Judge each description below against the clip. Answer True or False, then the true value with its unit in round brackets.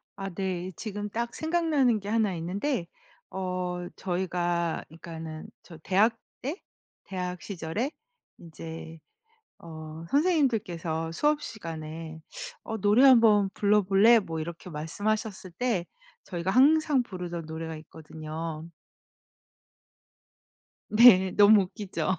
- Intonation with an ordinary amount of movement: True (5.0 semitones)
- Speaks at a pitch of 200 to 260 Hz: False (185 Hz)